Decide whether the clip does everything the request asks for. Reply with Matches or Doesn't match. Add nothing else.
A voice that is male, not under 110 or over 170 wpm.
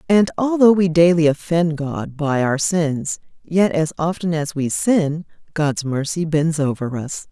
Doesn't match